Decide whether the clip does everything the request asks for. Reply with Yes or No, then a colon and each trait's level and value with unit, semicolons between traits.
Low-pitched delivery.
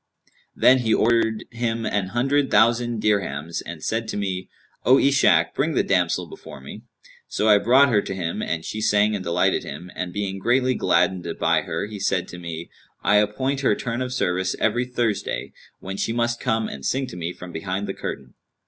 Yes: low, 105 Hz